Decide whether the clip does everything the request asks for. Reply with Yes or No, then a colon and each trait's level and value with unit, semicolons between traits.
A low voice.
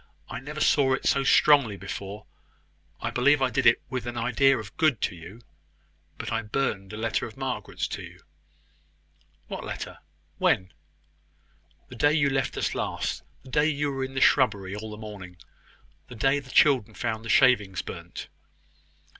Yes: low, 120 Hz